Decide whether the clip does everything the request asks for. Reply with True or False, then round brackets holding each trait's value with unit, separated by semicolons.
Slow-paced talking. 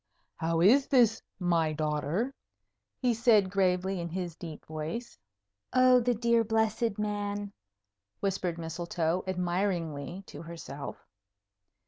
True (110 wpm)